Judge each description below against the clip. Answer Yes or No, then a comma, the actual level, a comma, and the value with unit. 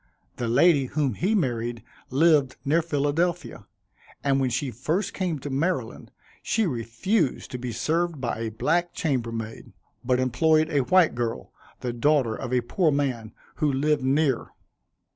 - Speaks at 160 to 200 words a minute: No, average, 150 wpm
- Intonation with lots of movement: No, average, 4.8 semitones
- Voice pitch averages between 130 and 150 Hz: Yes, medium, 140 Hz